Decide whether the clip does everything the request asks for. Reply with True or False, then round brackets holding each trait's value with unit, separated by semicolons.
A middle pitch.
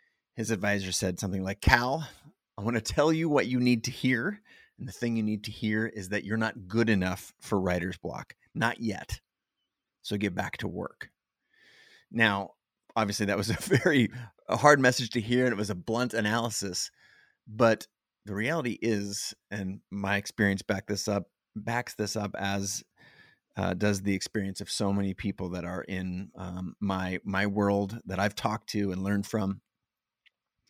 False (105 Hz)